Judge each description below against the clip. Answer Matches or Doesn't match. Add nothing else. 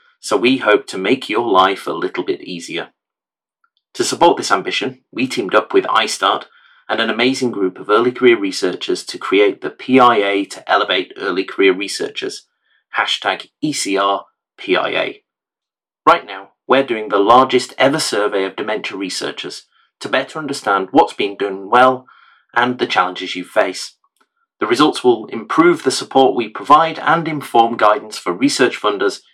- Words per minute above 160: Doesn't match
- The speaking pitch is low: Doesn't match